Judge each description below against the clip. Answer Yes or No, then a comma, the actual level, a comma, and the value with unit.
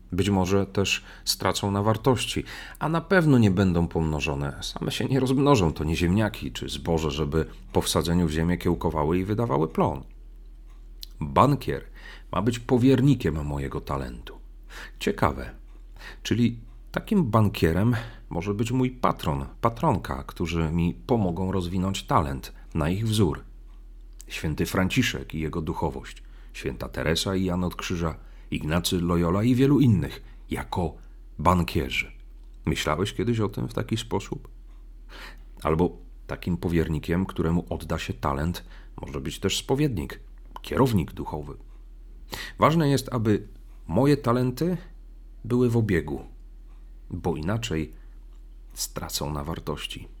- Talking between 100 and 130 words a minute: Yes, average, 125 wpm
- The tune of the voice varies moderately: No, wide, 6.1 semitones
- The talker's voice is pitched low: Yes, very low, 90 Hz